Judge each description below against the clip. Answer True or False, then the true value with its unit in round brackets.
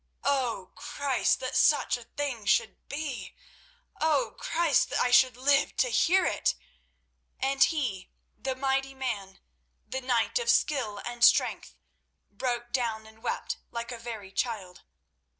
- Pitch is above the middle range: True (250 Hz)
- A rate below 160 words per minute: True (140 wpm)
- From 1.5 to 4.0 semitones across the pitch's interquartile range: True (3.4 semitones)